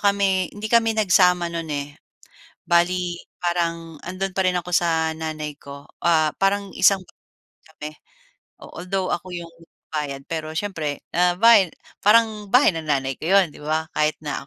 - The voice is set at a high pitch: No, medium, 175 Hz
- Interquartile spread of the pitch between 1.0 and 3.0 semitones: No, average, 3.5 semitones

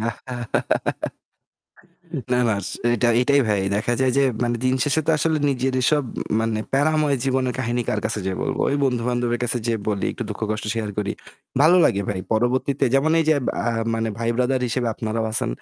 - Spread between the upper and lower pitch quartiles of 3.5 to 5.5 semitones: No, average, 3.0 semitones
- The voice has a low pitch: Yes, low, 120 Hz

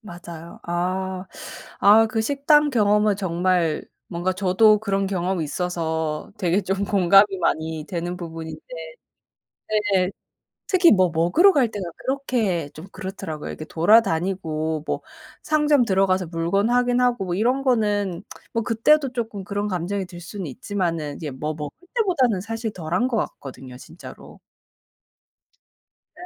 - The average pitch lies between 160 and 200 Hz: Yes, high, 190 Hz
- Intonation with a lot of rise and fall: No, average, 4.6 semitones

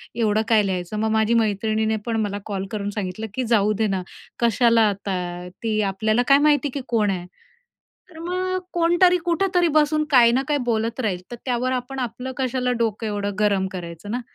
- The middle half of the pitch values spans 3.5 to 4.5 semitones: Yes, average, 4.0 semitones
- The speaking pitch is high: Yes, high, 225 Hz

